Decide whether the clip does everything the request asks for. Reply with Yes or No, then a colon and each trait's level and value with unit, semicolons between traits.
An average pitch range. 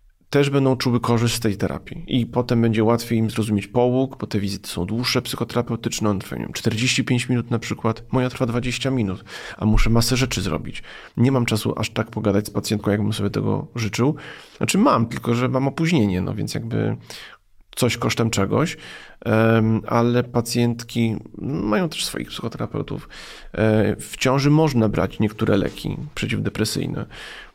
Yes: average, 3.0 semitones